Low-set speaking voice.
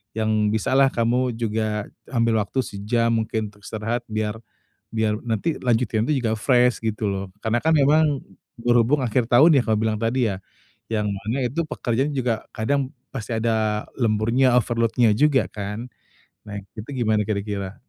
Yes: low, 115 Hz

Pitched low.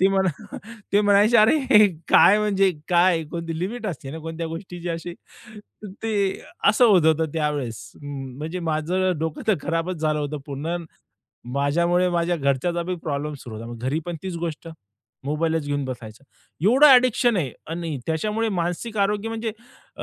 No: medium, 170 Hz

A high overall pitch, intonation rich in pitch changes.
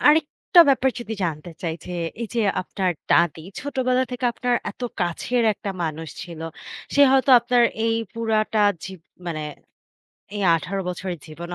Yes: high, 205 Hz; wide, 6.3 semitones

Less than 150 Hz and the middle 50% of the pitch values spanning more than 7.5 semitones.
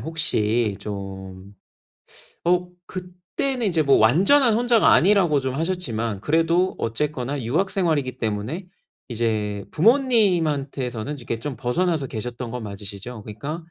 Yes: medium, 140 Hz; wide, 8.1 semitones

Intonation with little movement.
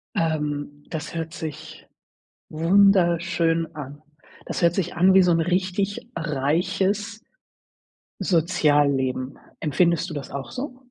No: average, 3.7 semitones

